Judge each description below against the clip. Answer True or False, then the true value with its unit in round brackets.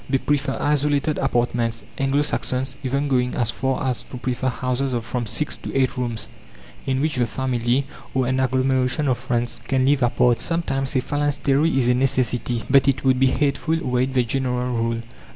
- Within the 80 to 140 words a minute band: False (190 wpm)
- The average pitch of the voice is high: False (130 Hz)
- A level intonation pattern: True (1.8 semitones)